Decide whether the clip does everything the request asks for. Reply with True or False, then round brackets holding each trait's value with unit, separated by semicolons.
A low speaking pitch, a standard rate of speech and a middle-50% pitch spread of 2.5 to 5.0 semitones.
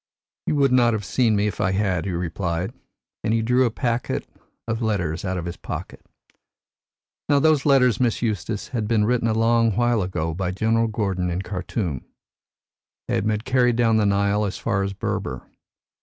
True (105 Hz; 185 wpm; 4.0 semitones)